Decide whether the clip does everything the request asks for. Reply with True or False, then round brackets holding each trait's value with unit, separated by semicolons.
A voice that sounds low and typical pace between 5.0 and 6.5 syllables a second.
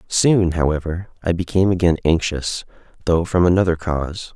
True (85 Hz; 5.3 syllables/s)